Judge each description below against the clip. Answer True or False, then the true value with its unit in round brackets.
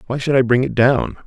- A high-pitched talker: False (130 Hz)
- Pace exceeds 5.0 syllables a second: True (5.8 syllables/s)